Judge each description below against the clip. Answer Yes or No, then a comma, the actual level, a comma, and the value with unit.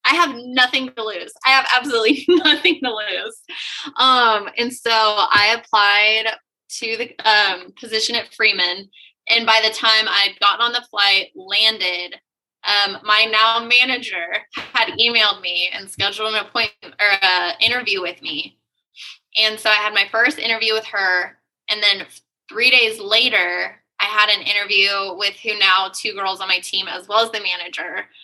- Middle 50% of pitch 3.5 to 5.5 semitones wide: No, average, 2.8 semitones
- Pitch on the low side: No, high, 220 Hz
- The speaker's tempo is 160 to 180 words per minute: Yes, average, 170 wpm